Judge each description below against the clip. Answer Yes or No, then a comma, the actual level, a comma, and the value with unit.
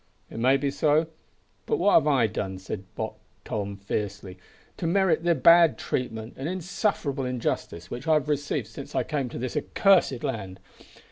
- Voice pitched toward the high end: No, low, 135 Hz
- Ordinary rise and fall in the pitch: No, wide, 6.9 semitones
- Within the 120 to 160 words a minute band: No, average, 175 wpm